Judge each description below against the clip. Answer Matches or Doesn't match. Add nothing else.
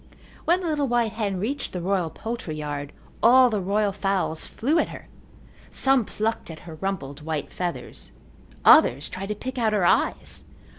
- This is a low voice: Doesn't match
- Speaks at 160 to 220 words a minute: Matches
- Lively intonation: Matches